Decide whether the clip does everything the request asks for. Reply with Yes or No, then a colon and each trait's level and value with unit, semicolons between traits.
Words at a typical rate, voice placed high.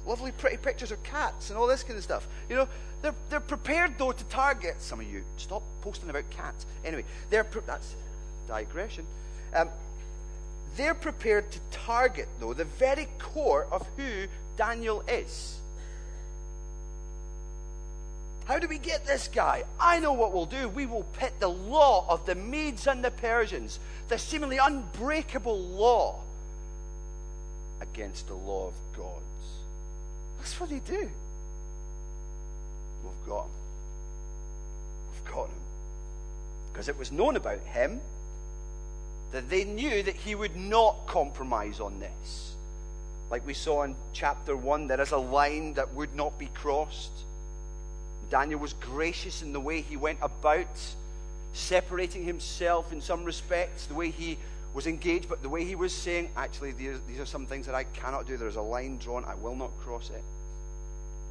No: average, 155 wpm; low, 135 Hz